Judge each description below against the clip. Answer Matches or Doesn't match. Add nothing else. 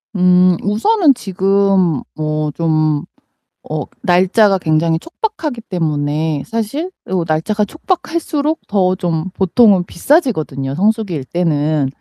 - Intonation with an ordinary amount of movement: Doesn't match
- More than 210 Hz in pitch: Doesn't match